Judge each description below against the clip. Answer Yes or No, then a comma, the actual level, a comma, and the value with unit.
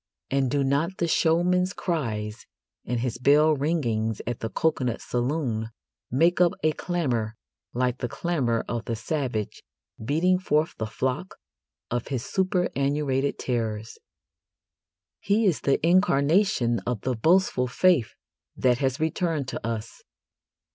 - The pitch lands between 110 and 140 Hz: Yes, low, 135 Hz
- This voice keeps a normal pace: No, slow, 130 wpm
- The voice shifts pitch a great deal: Yes, wide, 5.8 semitones